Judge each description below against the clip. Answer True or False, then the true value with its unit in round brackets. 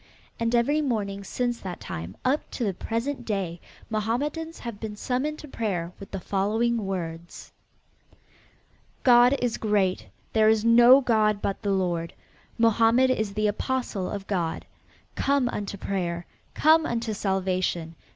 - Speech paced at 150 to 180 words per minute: False (140 wpm)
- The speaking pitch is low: False (215 Hz)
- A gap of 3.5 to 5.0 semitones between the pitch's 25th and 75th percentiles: True (4.0 semitones)